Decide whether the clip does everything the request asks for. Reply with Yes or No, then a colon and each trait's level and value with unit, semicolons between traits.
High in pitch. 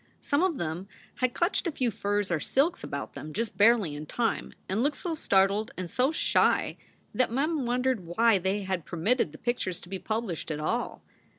Yes: high, 215 Hz